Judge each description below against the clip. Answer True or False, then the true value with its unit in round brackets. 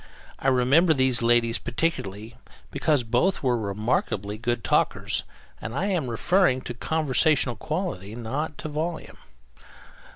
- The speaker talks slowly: True (125 wpm)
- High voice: False (125 Hz)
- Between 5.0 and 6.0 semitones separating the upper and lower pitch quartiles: True (5.3 semitones)